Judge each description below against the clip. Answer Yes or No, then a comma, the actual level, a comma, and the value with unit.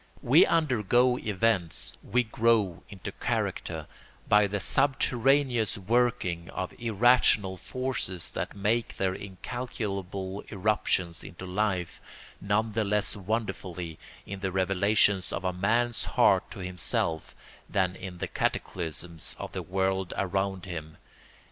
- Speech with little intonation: No, average, 3.6 semitones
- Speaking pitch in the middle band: No, low, 100 Hz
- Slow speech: Yes, slow, 120 wpm